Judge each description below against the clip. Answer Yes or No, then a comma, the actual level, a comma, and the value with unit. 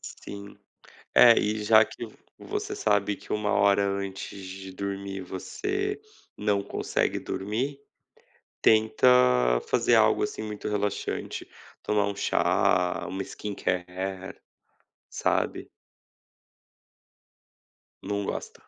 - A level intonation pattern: Yes, narrow, 1.7 semitones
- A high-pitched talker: No, low, 100 Hz